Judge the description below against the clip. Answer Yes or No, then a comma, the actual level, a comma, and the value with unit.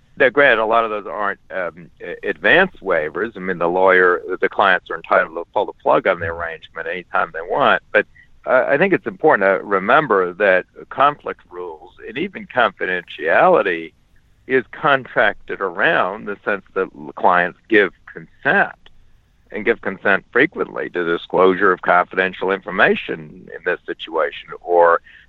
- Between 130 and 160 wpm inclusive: Yes, average, 150 wpm